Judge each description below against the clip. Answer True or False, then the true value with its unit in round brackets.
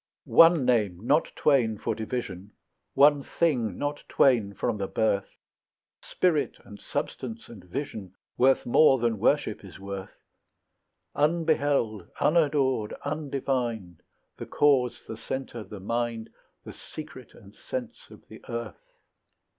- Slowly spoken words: True (125 wpm)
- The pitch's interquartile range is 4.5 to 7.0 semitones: True (5.1 semitones)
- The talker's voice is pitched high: False (120 Hz)